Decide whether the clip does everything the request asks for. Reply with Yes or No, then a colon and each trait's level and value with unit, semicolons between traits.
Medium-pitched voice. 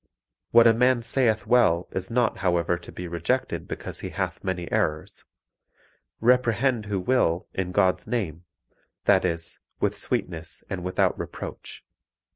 No: very low, 95 Hz